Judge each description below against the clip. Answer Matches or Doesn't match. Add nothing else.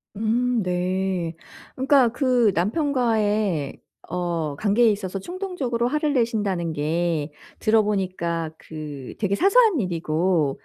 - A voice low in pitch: Doesn't match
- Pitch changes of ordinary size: Doesn't match